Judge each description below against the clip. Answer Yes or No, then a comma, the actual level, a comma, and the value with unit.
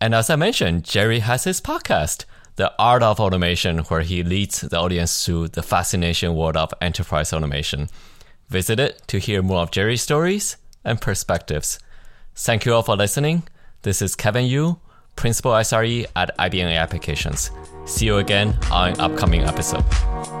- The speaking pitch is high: No, very low, 95 Hz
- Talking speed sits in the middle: Yes, average, 160 wpm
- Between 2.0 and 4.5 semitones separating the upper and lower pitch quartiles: No, average, 5.3 semitones